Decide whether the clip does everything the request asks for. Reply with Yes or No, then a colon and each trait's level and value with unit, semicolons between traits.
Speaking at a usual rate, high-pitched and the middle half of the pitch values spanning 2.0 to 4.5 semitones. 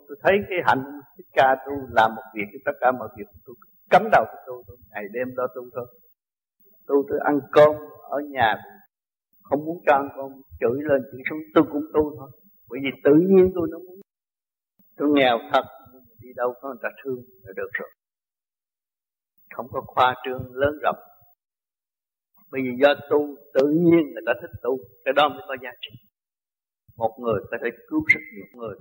No: average, 200 wpm; medium, 140 Hz; average, 3.6 semitones